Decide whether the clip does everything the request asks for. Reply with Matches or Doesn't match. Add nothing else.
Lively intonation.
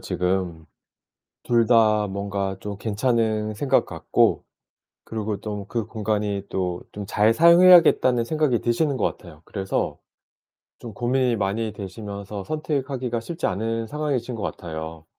Doesn't match